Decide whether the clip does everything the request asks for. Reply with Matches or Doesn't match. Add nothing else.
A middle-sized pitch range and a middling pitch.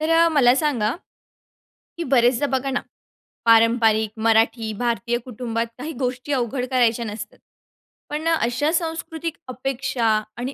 Doesn't match